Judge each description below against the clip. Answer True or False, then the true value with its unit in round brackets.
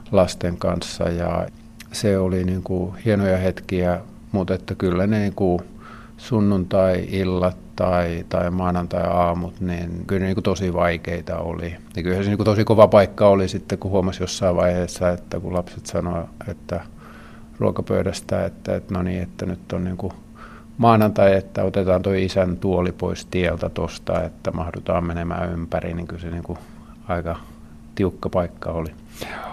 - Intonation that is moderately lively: False (2.2 semitones)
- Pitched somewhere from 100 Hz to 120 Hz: False (90 Hz)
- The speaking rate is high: True (160 wpm)